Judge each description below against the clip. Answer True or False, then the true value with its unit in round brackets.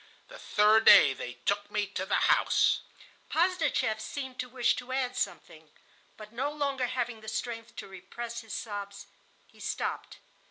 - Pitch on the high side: True (230 Hz)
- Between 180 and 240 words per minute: False (160 wpm)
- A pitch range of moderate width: True (3.8 semitones)